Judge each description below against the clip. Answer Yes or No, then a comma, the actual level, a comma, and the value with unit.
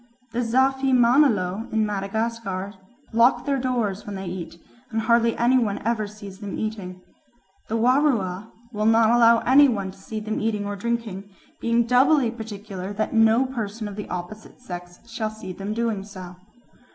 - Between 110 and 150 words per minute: No, average, 165 wpm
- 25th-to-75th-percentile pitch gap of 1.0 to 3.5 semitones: Yes, average, 2.9 semitones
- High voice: Yes, high, 220 Hz